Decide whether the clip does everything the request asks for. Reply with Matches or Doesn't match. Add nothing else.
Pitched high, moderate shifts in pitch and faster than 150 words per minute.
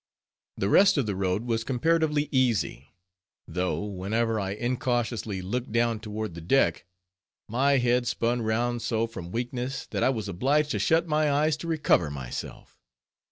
Doesn't match